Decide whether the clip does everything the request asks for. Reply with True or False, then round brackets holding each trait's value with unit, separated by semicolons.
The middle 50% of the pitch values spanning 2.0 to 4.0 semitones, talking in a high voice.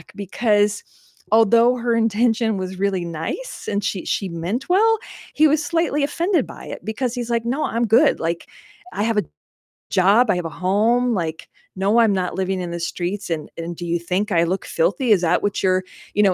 False (4.6 semitones; 205 Hz)